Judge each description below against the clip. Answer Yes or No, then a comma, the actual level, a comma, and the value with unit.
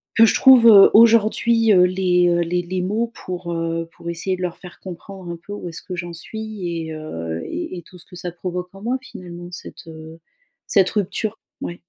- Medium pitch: Yes, medium, 180 Hz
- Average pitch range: Yes, average, 3.1 semitones